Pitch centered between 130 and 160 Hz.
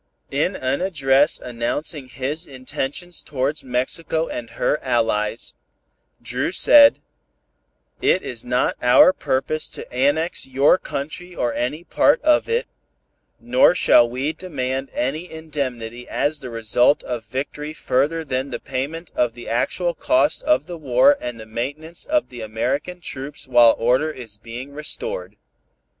Yes: low, 135 Hz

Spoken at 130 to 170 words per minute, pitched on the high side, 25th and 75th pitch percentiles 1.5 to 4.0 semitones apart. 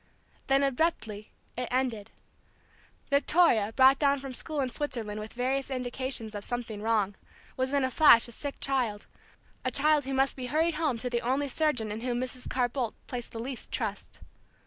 No: average, 180 wpm; very high, 255 Hz; average, 3.0 semitones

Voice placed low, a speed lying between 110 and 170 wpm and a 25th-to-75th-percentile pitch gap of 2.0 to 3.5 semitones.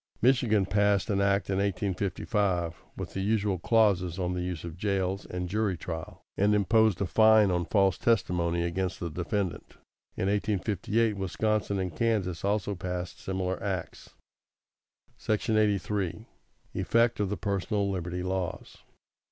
Yes: very low, 95 Hz; average, 145 wpm; narrow, 2.6 semitones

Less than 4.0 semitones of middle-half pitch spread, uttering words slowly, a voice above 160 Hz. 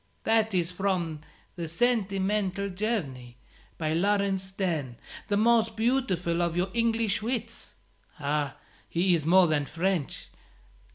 No: average, 4.5 semitones; slow, 120 wpm; high, 190 Hz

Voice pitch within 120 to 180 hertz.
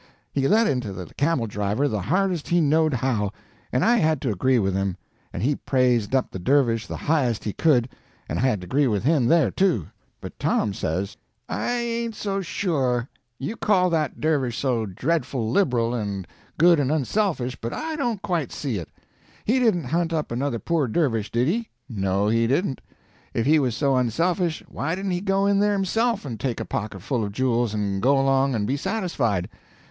Yes: low, 135 Hz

